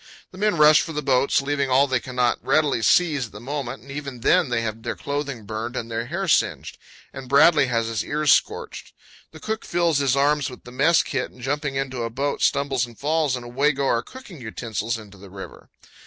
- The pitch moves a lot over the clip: No, average, 3.8 semitones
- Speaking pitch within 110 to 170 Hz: Yes, low, 135 Hz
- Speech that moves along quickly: Yes, fast, 215 wpm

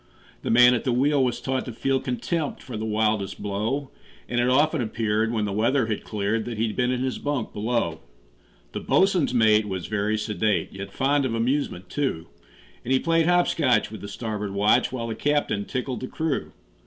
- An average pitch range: Yes, average, 3.8 semitones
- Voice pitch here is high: No, low, 120 Hz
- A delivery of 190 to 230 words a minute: Yes, average, 200 wpm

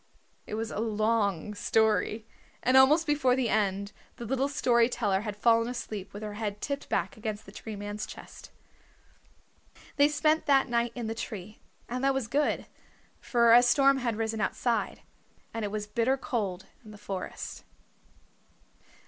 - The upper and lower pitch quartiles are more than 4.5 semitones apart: No, average, 3.3 semitones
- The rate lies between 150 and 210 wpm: Yes, average, 165 wpm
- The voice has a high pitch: Yes, high, 230 Hz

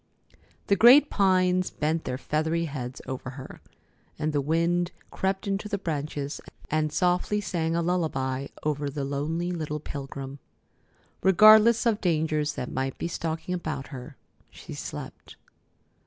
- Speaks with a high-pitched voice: No, medium, 160 Hz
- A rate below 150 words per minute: Yes, average, 140 wpm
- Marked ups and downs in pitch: No, average, 4.1 semitones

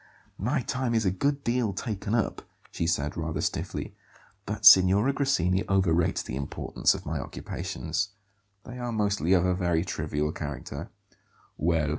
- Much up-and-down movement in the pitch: Yes, wide, 5.9 semitones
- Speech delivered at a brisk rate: No, average, 145 wpm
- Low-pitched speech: Yes, very low, 95 Hz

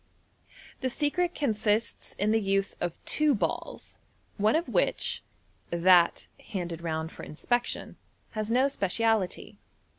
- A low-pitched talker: No, high, 215 Hz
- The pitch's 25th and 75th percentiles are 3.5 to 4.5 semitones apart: No, average, 5.2 semitones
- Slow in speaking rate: Yes, slow, 120 wpm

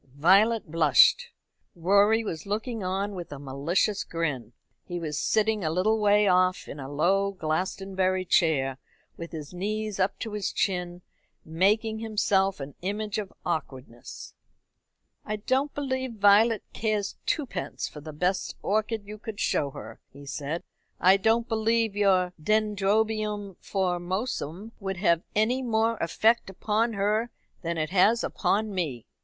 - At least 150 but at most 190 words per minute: No, average, 140 wpm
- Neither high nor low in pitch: No, high, 195 Hz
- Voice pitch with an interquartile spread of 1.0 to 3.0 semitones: No, average, 4.1 semitones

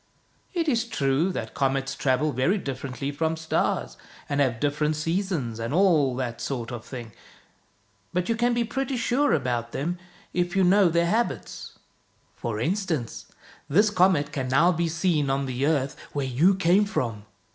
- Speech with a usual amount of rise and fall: No, wide, 6.1 semitones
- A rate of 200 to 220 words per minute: No, average, 165 wpm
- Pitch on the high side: No, medium, 150 Hz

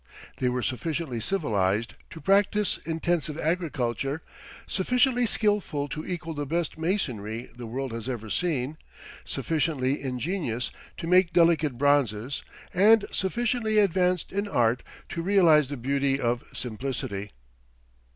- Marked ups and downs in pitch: Yes, wide, 6.3 semitones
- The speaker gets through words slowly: Yes, slow, 120 wpm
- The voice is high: No, medium, 150 Hz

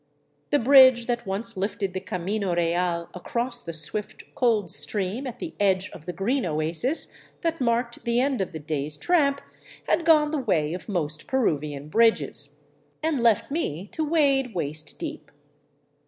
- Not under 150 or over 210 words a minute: Yes, average, 160 wpm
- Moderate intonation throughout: No, wide, 7.6 semitones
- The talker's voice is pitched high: Yes, high, 210 Hz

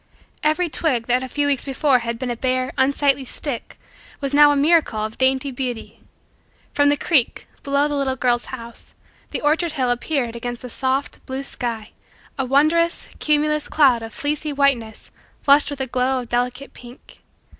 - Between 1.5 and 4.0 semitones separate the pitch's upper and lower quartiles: Yes, average, 2.8 semitones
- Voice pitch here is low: No, very high, 265 Hz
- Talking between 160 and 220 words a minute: Yes, average, 175 wpm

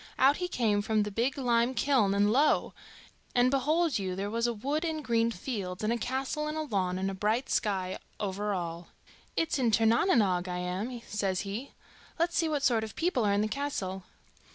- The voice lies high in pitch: Yes, high, 225 Hz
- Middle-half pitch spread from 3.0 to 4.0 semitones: No, wide, 5.4 semitones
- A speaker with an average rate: No, fast, 215 wpm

